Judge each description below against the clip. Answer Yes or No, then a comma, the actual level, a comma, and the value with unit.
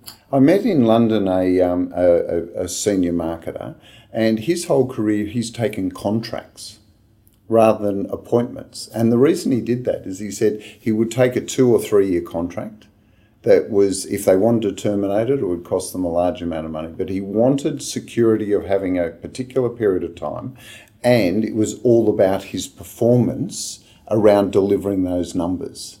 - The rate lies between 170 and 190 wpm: Yes, average, 180 wpm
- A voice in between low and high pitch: No, low, 105 Hz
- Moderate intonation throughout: Yes, average, 3.3 semitones